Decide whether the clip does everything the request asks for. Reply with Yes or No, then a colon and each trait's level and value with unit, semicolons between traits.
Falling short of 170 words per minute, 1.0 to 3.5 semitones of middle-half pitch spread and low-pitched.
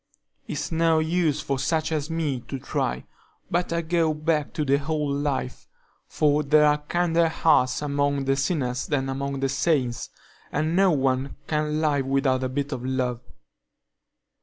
No: average, 160 wpm; average, 2.7 semitones; medium, 145 Hz